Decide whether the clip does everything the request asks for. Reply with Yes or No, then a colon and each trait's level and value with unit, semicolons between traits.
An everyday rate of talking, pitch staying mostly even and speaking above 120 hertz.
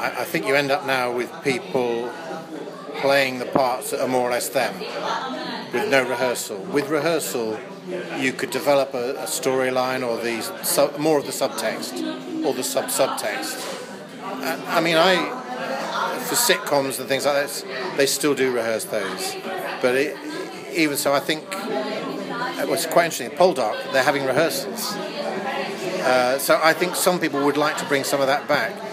No: average, 170 wpm; average, 3.9 semitones; medium, 140 Hz